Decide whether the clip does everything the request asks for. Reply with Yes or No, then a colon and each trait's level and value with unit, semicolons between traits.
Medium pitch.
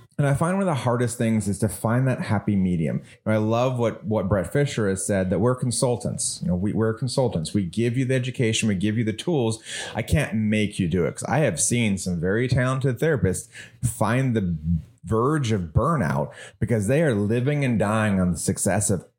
No: low, 115 Hz